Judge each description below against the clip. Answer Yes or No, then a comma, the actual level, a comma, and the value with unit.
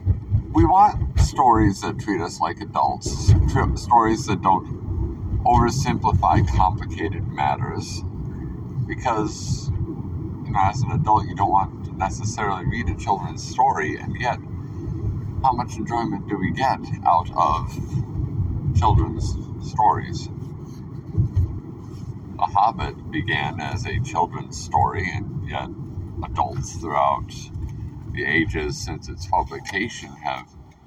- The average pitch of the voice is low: Yes, low, 105 Hz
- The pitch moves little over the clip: No, average, 3.2 semitones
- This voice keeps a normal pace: No, slow, 115 wpm